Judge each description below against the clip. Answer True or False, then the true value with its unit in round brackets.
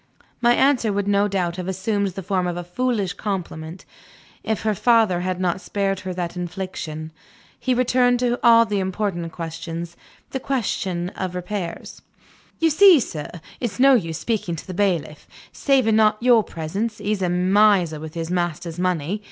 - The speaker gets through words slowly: False (165 wpm)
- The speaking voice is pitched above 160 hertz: True (190 Hz)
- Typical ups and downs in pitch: True (4.1 semitones)